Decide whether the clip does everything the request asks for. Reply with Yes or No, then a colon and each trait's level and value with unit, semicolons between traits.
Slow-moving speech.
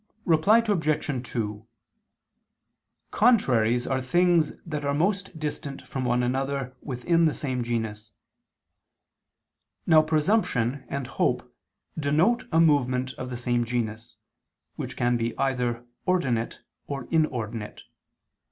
Yes: slow, 115 wpm